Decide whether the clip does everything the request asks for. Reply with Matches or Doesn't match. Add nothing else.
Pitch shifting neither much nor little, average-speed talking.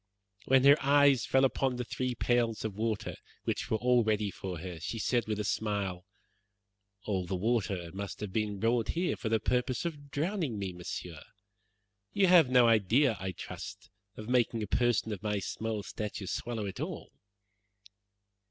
Matches